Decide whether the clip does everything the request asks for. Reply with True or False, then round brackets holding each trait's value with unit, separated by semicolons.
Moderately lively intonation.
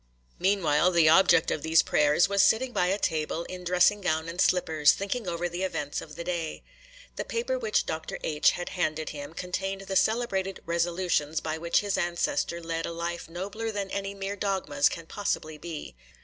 True (3.4 semitones)